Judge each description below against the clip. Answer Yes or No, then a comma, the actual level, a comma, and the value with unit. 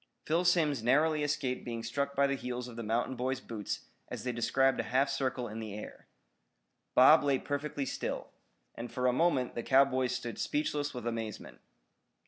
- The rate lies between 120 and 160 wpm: No, average, 180 wpm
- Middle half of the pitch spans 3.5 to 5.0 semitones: No, average, 3.0 semitones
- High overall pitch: No, low, 130 Hz